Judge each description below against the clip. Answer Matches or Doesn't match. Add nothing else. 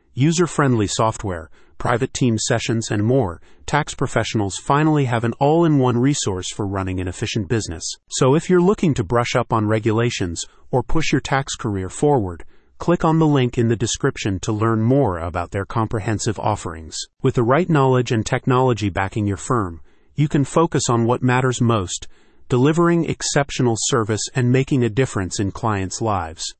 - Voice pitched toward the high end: Doesn't match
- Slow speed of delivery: Doesn't match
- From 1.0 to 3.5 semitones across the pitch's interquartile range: Doesn't match